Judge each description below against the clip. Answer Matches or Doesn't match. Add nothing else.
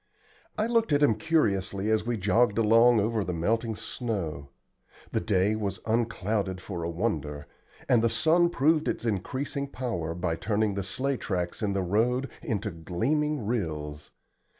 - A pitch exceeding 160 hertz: Doesn't match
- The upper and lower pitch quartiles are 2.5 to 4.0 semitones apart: Doesn't match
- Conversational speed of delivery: Matches